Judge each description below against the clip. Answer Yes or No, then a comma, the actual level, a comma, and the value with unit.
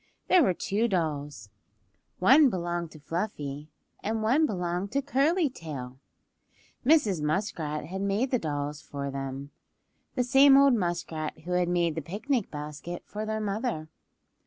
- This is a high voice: No, medium, 180 Hz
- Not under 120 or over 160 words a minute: Yes, average, 140 wpm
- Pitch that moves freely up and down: Yes, wide, 7.3 semitones